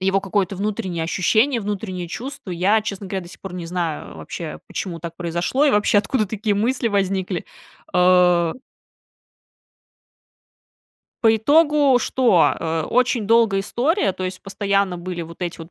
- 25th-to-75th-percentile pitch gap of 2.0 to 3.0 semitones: No, average, 3.7 semitones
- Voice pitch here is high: Yes, high, 195 Hz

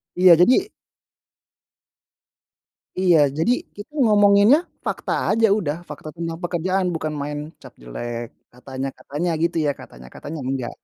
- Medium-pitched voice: Yes, medium, 170 Hz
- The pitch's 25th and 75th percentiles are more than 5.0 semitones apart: Yes, wide, 5.6 semitones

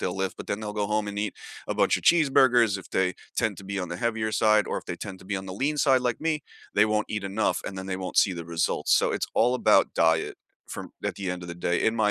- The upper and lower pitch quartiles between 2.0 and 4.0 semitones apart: Yes, average, 3.0 semitones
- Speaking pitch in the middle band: No, low, 105 Hz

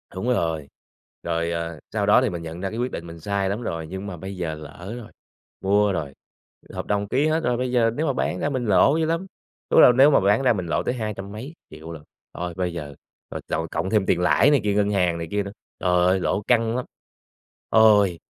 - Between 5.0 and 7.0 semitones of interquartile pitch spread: Yes, average, 5.3 semitones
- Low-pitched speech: Yes, low, 100 Hz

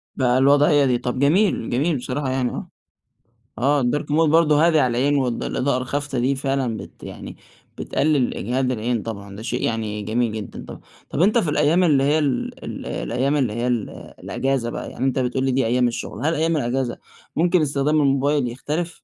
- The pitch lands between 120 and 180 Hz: Yes, low, 135 Hz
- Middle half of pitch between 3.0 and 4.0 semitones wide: Yes, average, 3.3 semitones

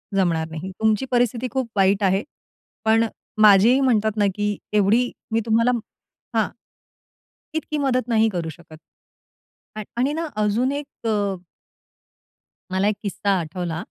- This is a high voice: Yes, high, 215 Hz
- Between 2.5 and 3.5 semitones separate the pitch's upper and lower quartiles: No, average, 4.0 semitones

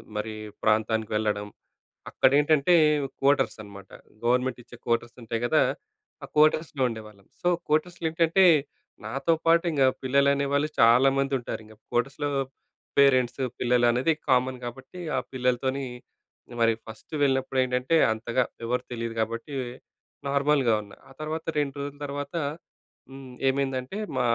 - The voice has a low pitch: Yes, low, 130 Hz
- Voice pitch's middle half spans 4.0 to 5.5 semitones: No, average, 3.2 semitones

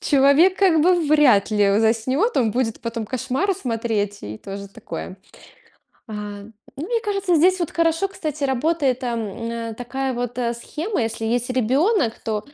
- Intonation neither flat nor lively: No, wide, 6.3 semitones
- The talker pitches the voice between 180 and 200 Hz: No, very high, 255 Hz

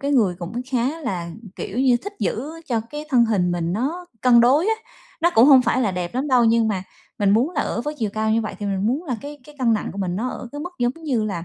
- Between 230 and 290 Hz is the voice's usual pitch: Yes, high, 235 Hz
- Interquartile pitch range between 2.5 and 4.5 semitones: No, average, 5.2 semitones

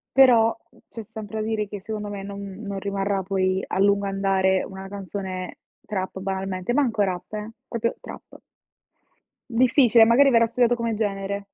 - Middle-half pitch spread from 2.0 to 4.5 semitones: Yes, average, 2.7 semitones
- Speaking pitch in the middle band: No, high, 200 Hz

